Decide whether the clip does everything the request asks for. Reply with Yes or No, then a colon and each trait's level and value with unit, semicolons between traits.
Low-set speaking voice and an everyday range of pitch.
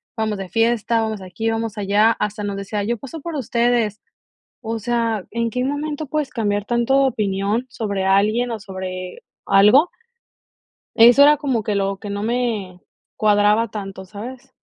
No: high, 220 Hz; average, 3.0 semitones